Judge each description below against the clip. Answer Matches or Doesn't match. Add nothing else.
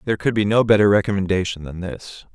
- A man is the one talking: Matches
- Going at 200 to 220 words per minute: Matches